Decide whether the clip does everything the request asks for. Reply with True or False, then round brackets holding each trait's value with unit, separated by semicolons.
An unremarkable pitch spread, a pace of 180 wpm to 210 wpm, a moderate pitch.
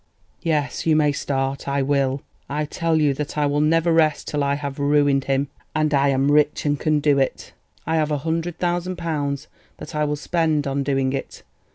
False (1.9 semitones; 200 wpm; 145 Hz)